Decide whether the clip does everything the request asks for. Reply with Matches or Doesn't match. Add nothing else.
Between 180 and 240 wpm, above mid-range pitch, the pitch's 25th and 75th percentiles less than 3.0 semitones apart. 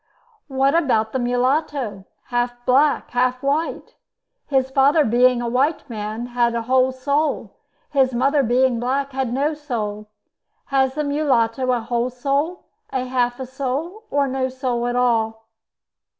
Doesn't match